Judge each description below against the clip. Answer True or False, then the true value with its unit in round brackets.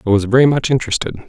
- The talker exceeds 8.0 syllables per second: True (9.0 syllables/s)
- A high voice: False (120 Hz)